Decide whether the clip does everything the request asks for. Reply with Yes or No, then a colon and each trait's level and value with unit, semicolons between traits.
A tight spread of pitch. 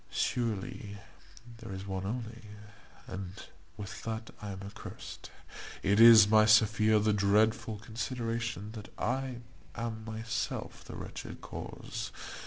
Yes: narrow, 2.1 semitones